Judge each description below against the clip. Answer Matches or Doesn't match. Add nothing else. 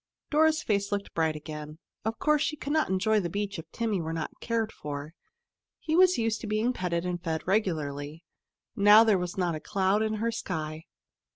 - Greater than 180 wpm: Matches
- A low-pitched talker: Doesn't match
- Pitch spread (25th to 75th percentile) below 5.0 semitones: Doesn't match